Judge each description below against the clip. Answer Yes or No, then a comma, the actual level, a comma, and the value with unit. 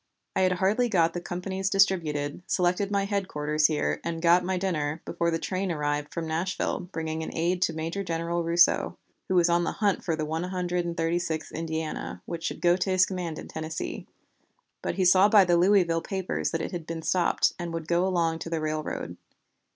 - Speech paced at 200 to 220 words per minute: Yes, fast, 205 wpm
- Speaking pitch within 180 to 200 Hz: No, medium, 170 Hz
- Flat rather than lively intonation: Yes, narrow, 2.3 semitones